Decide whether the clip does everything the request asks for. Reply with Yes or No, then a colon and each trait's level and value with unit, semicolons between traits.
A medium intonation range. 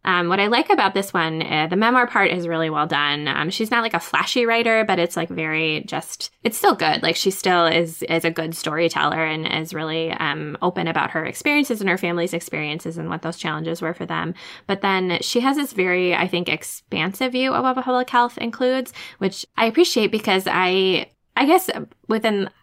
No: wide, 5.8 semitones